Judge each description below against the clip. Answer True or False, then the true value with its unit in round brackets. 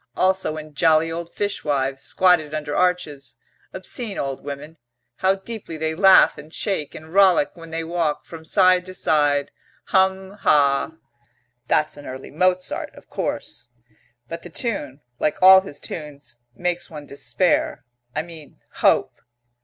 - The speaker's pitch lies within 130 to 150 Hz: False (160 Hz)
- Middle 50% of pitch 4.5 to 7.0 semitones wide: False (4.0 semitones)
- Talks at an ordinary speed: True (145 wpm)